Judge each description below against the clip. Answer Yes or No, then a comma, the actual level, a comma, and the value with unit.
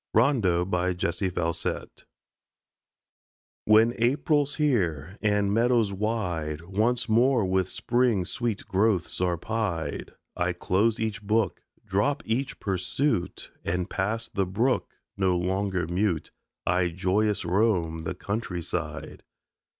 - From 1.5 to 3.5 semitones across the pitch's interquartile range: No, average, 4.2 semitones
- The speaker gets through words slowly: Yes, slow, 110 wpm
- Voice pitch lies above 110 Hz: No, low, 100 Hz